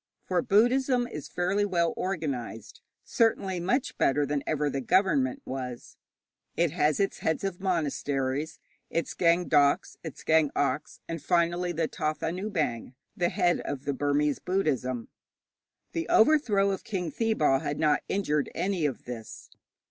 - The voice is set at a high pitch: No, medium, 165 Hz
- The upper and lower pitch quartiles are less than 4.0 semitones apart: No, average, 4.8 semitones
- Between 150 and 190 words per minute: No, average, 140 wpm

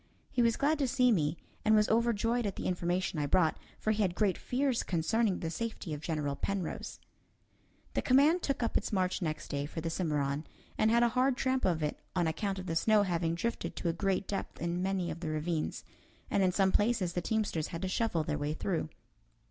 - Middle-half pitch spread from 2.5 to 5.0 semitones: No, wide, 5.6 semitones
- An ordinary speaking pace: No, fast, 220 wpm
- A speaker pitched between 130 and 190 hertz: Yes, medium, 185 Hz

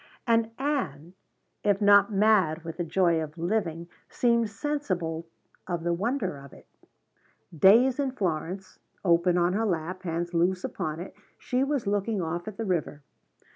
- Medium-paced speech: Yes, average, 155 wpm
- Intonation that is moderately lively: Yes, average, 4.6 semitones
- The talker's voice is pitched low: No, medium, 185 Hz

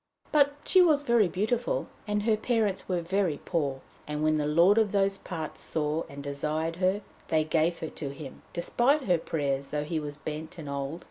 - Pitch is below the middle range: No, medium, 165 Hz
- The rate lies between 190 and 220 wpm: Yes, average, 195 wpm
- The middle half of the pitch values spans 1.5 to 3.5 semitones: No, wide, 5.4 semitones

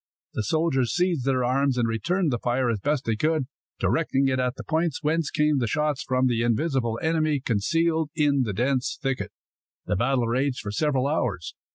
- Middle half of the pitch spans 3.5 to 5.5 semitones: Yes, average, 4.0 semitones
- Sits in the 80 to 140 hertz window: Yes, low, 135 Hz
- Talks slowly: No, average, 190 wpm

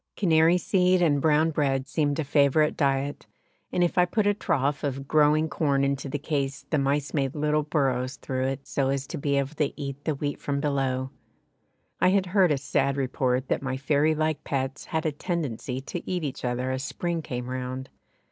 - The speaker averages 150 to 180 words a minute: No, average, 200 wpm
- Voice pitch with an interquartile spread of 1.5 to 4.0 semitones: Yes, narrow, 2.6 semitones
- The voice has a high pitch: No, medium, 145 Hz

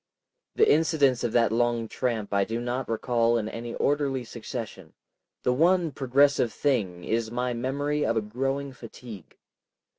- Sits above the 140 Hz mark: No, low, 120 Hz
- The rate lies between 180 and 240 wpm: No, average, 150 wpm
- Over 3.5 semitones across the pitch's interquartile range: No, average, 3.1 semitones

